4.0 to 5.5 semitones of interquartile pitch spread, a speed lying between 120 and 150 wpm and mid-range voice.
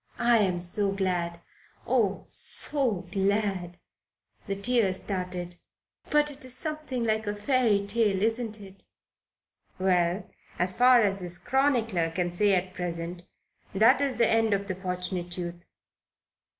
No: average, 4.3 semitones; slow, 135 wpm; high, 200 Hz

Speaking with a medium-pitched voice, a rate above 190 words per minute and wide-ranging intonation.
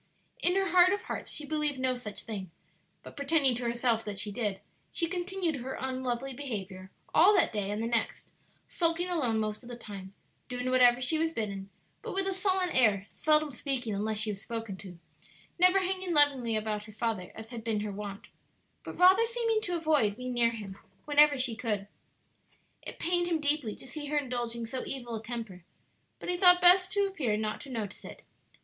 No: very high, 250 Hz; average, 200 wpm; wide, 7.1 semitones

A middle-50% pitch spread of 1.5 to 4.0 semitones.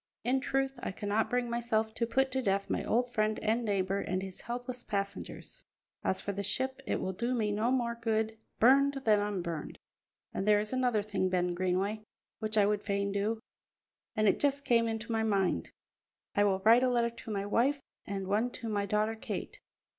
Yes: average, 3.1 semitones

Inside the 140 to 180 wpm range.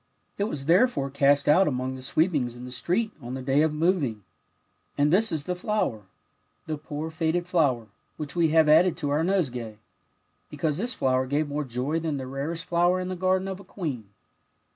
No: average, 195 wpm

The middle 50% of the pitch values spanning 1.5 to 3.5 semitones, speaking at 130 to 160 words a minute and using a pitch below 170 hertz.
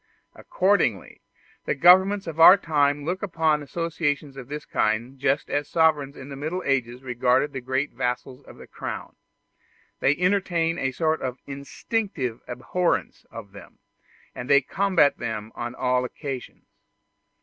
No: average, 4.6 semitones; average, 145 wpm; medium, 140 Hz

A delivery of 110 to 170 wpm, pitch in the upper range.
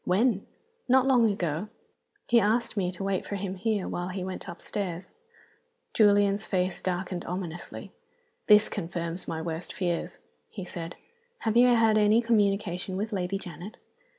Yes: average, 150 wpm; high, 195 Hz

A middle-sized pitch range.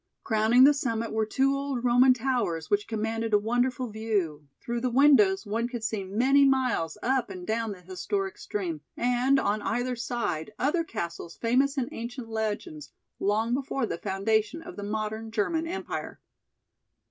Yes: average, 3.8 semitones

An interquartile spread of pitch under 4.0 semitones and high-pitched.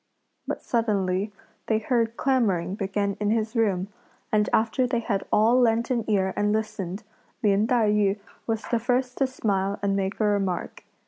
Yes: average, 2.7 semitones; high, 215 Hz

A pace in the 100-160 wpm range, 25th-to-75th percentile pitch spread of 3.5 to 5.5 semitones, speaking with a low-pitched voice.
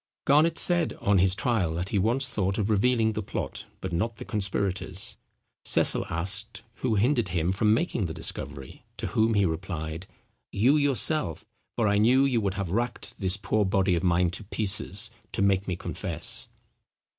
No: average, 175 wpm; average, 4.0 semitones; low, 100 Hz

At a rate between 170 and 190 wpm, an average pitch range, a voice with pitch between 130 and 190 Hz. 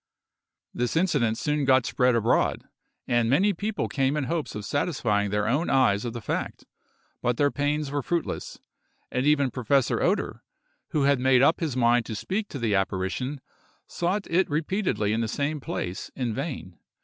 Yes: average, 175 wpm; average, 4.4 semitones; low, 135 Hz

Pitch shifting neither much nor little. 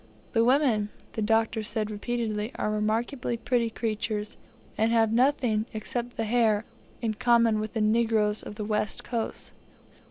No: narrow, 1.7 semitones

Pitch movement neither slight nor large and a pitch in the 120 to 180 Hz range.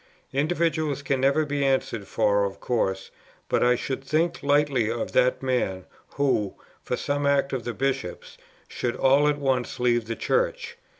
Yes: average, 3.2 semitones; low, 135 Hz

